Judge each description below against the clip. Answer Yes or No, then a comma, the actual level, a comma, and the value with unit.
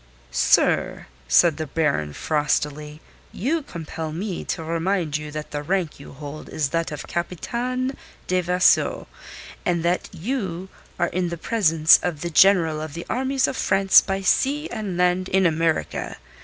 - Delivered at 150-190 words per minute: Yes, average, 155 wpm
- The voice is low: No, medium, 170 Hz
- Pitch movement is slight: No, average, 3.7 semitones